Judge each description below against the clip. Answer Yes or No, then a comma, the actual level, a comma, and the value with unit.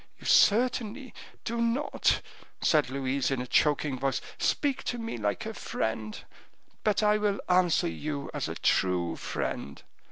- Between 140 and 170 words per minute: Yes, average, 150 wpm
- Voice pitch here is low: No, medium, 150 Hz